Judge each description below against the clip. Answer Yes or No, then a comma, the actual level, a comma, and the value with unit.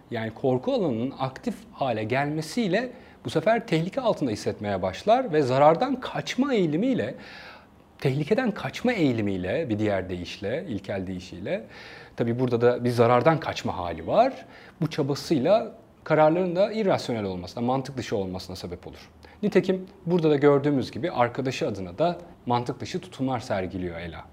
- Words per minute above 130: Yes, fast, 140 wpm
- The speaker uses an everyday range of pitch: No, wide, 8.8 semitones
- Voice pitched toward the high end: No, low, 135 Hz